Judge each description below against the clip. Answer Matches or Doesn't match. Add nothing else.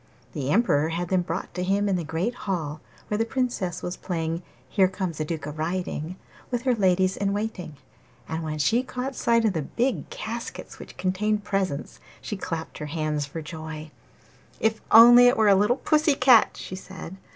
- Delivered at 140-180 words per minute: Doesn't match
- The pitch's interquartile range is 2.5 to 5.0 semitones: Doesn't match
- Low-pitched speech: Doesn't match